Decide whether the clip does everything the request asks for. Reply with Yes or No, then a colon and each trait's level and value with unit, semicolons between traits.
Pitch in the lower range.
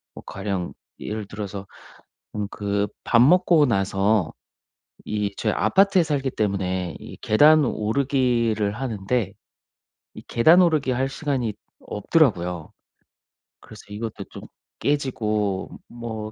Yes: low, 110 Hz